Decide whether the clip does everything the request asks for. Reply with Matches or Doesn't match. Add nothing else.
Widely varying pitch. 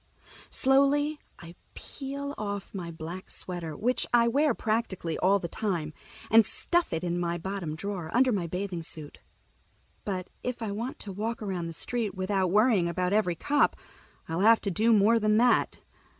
Doesn't match